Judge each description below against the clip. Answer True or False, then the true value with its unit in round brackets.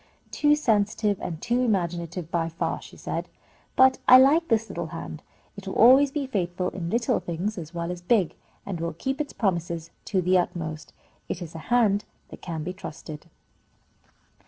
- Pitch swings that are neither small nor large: False (5.7 semitones)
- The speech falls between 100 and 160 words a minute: False (180 wpm)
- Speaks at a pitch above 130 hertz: True (185 Hz)